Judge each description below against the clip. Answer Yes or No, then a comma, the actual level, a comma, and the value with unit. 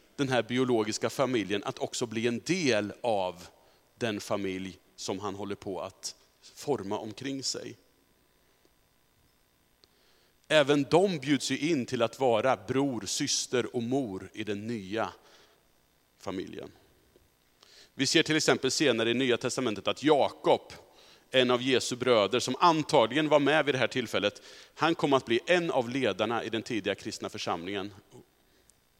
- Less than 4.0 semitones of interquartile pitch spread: No, average, 5.2 semitones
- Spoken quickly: No, average, 145 wpm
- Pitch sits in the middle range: No, low, 125 Hz